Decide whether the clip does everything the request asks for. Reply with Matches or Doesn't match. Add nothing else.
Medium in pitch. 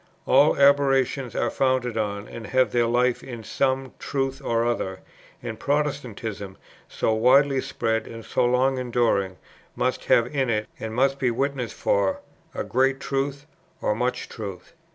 Doesn't match